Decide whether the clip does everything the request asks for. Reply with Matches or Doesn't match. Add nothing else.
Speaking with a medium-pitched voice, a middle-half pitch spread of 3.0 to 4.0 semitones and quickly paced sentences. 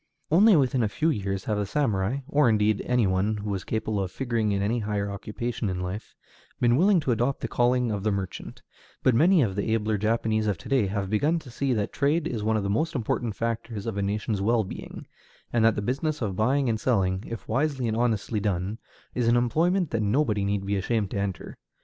Doesn't match